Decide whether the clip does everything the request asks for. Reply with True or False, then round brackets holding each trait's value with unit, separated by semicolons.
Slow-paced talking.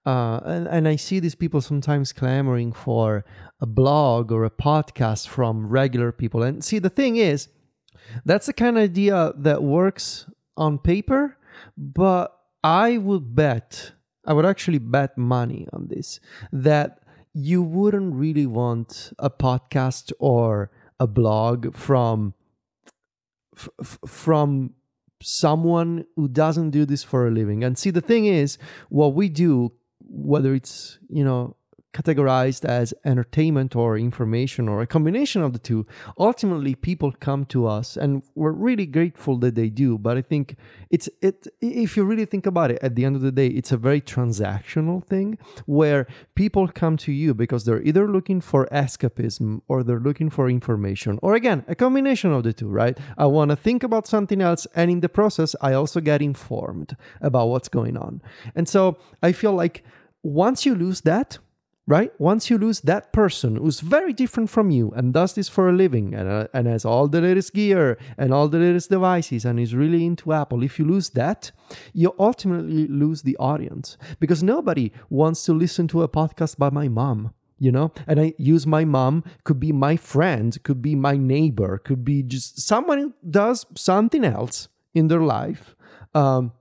False (175 wpm)